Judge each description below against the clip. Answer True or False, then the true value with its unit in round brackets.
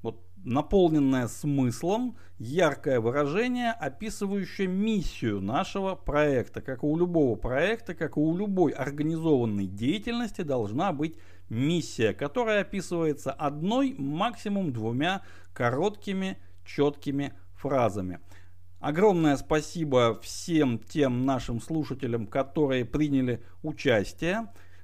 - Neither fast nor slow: False (95 wpm)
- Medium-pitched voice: True (145 Hz)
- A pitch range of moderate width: False (7.3 semitones)